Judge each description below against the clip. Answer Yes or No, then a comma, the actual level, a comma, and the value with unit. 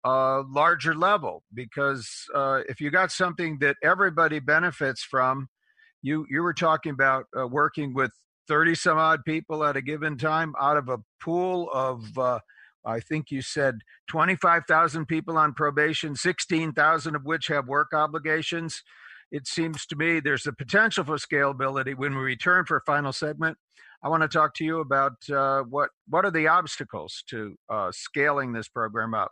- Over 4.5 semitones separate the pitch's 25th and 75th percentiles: No, average, 3.1 semitones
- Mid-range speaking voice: Yes, medium, 150 Hz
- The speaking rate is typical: Yes, average, 180 wpm